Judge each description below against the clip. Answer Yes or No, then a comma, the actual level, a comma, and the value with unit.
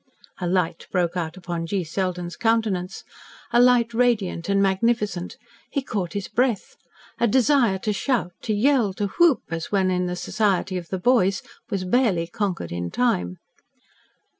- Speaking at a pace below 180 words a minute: Yes, average, 160 wpm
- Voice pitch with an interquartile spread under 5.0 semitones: Yes, average, 4.4 semitones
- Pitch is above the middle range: Yes, high, 195 Hz